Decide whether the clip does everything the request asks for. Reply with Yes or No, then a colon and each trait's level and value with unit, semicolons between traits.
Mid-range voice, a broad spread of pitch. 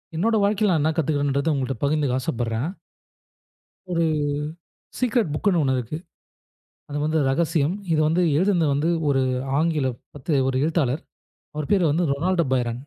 No: medium, 155 Hz; average, 3.9 semitones